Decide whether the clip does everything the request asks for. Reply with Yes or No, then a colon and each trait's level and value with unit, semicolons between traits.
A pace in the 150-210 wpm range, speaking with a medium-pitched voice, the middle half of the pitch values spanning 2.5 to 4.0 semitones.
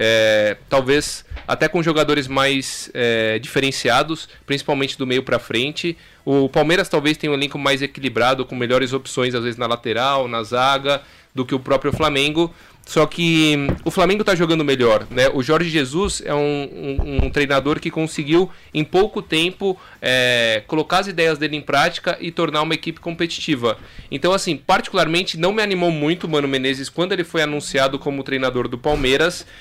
Yes: average, 175 wpm; medium, 145 Hz; average, 3.6 semitones